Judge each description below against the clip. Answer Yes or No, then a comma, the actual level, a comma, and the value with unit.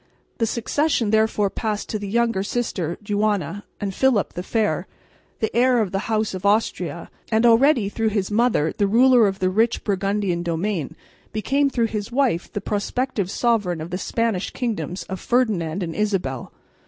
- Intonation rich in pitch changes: No, average, 3.3 semitones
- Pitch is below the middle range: No, high, 210 Hz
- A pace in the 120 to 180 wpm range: Yes, average, 165 wpm